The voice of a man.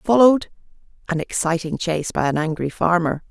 No: female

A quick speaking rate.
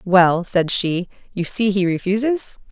No: average, 155 wpm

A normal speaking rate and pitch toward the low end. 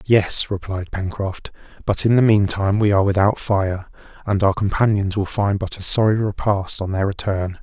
Yes: average, 180 wpm; low, 100 Hz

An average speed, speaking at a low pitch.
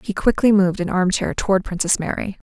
No: average, 195 wpm; high, 190 Hz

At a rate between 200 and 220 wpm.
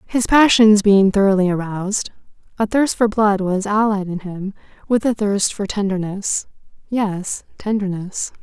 No: slow, 135 wpm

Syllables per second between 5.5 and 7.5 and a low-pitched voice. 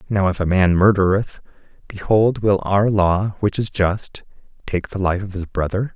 No: 4.5 syllables/s; low, 100 Hz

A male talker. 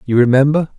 Yes: male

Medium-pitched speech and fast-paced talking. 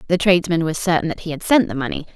Yes: medium, 170 Hz; fast, 280 wpm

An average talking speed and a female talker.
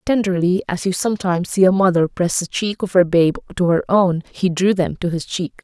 No: fast, 235 wpm; female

